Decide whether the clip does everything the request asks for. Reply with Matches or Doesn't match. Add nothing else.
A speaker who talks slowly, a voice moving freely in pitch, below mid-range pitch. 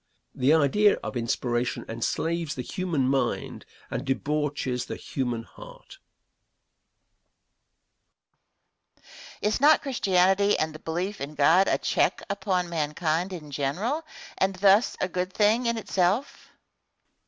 Doesn't match